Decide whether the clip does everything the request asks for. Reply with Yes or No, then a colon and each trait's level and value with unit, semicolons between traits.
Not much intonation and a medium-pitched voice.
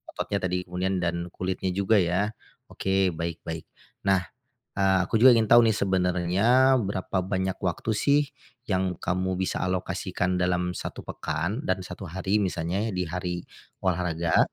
No: narrow, 1.7 semitones; very low, 95 Hz